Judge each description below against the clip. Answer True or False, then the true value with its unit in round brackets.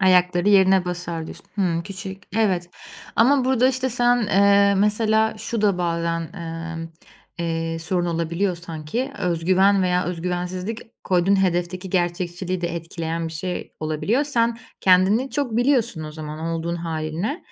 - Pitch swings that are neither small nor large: True (3.5 semitones)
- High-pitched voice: False (180 Hz)